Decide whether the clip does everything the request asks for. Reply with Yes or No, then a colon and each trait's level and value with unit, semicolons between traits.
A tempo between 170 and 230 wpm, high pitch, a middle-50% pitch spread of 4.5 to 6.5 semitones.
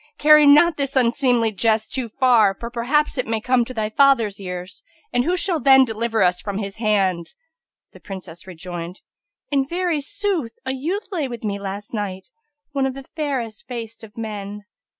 Yes: average, 180 wpm; high, 235 Hz; average, 5.2 semitones